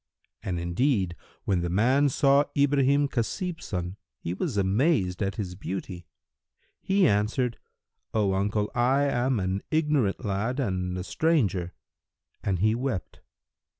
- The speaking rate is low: Yes, slow, 130 wpm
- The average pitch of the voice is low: Yes, low, 105 Hz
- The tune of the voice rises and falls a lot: Yes, wide, 6.6 semitones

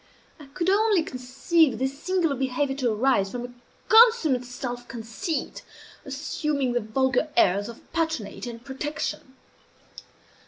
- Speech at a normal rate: No, slow, 125 wpm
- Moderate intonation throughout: Yes, average, 4.3 semitones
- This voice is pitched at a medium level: No, very high, 265 Hz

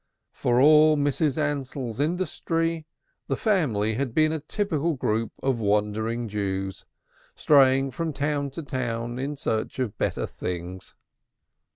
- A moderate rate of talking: No, slow, 130 wpm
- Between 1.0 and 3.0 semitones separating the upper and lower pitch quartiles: No, average, 5.3 semitones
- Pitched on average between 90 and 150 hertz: Yes, low, 135 Hz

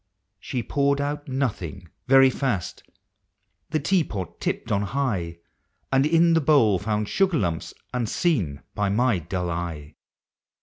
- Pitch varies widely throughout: Yes, wide, 7.0 semitones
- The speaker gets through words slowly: No, average, 145 wpm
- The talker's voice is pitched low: Yes, low, 125 Hz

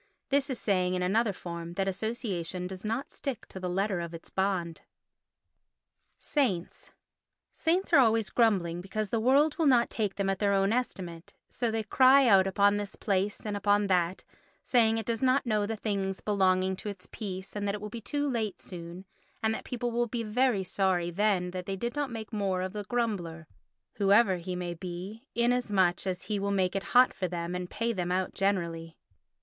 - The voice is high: Yes, high, 200 Hz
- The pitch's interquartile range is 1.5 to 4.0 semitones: Yes, average, 3.7 semitones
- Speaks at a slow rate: No, average, 200 wpm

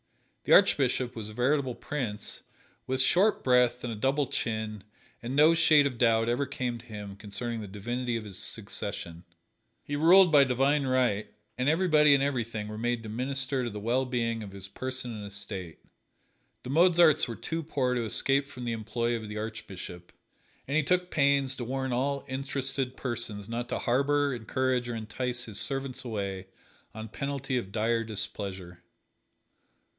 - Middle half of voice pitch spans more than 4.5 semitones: No, average, 4.0 semitones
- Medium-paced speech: Yes, average, 170 wpm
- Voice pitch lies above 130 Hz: No, low, 125 Hz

